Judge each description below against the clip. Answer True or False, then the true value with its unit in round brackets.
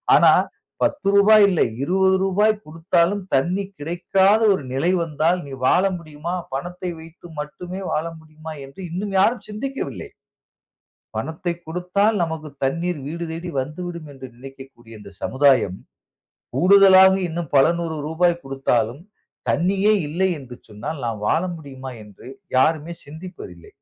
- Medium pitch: True (165 Hz)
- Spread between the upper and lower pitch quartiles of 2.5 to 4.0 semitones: False (5.1 semitones)